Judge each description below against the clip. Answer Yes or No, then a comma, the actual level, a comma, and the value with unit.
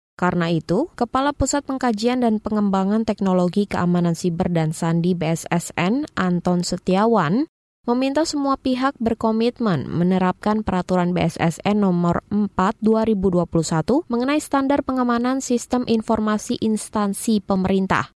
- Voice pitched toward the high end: Yes, high, 210 Hz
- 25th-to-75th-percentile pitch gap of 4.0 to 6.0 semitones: Yes, average, 5.1 semitones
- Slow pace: No, average, 100 wpm